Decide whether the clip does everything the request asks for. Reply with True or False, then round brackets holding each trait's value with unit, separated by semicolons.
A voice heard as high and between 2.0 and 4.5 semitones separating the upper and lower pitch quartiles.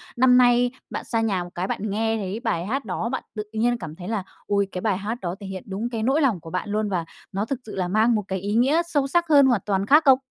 True (215 Hz; 4.2 semitones)